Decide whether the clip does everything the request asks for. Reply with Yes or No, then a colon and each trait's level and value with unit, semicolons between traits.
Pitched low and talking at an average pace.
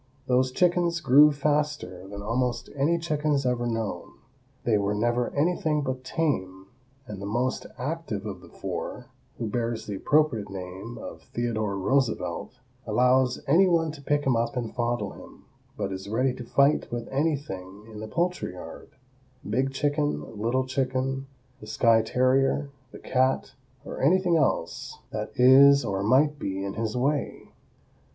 Yes: low, 130 Hz; average, 150 wpm